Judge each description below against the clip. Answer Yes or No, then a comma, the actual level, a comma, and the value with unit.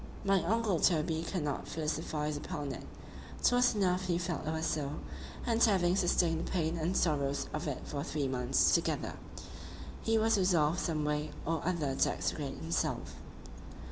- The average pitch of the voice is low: No, medium, 160 Hz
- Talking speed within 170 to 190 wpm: No, average, 155 wpm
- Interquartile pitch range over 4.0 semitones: No, average, 3.6 semitones